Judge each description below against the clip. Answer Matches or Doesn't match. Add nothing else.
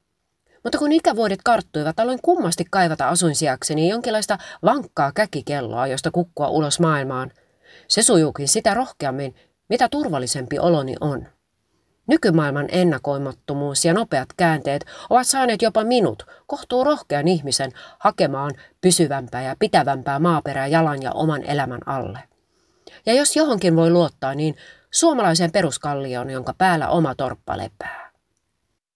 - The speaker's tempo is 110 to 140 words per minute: Matches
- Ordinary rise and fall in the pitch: Doesn't match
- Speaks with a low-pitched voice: Doesn't match